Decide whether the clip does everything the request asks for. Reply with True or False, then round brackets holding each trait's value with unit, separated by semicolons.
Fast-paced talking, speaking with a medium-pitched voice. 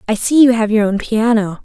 False (255 wpm; 220 Hz)